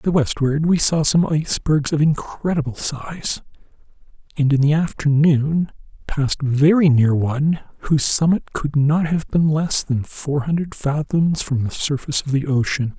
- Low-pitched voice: No, medium, 150 Hz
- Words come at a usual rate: Yes, average, 160 wpm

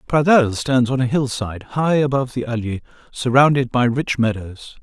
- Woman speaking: No, male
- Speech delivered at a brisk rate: No, average, 160 wpm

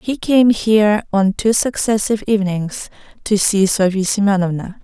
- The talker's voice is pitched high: Yes, high, 205 Hz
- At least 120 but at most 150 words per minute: Yes, slow, 135 wpm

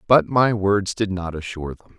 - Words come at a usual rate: No, fast, 210 wpm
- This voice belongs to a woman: No, male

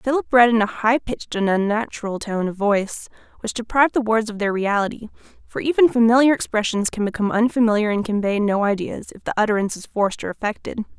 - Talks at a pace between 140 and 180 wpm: No, average, 195 wpm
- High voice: Yes, high, 220 Hz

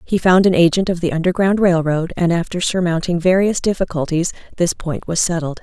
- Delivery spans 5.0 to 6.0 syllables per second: Yes, 5.5 syllables/s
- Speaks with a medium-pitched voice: Yes, medium, 175 Hz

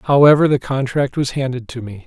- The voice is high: No, low, 135 Hz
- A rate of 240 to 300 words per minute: No, fast, 205 wpm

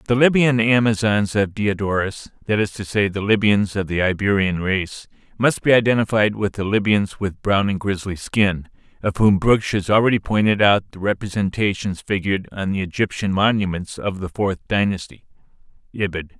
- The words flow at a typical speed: Yes, average, 155 wpm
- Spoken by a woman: No, male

